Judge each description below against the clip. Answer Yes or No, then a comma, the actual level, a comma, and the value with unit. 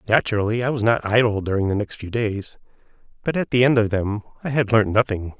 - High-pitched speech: No, low, 110 Hz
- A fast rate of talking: Yes, fast, 220 wpm